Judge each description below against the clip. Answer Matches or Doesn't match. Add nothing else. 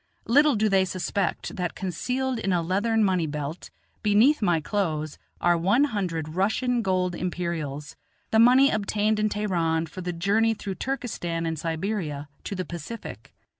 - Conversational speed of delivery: Matches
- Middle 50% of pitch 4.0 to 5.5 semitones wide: Matches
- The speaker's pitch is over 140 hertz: Matches